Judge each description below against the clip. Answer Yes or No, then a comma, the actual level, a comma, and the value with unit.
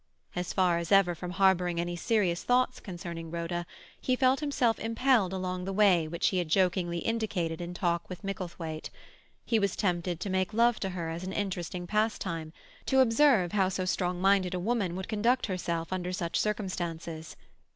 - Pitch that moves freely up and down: No, average, 3.3 semitones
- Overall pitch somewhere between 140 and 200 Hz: Yes, medium, 185 Hz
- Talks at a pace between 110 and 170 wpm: No, average, 180 wpm